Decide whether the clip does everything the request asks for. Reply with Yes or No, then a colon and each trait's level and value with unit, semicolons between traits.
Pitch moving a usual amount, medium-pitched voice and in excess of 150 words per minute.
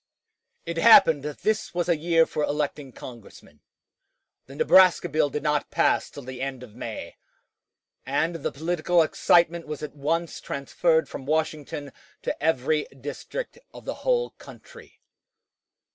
No: average, 3.2 semitones; medium, 155 Hz; average, 145 wpm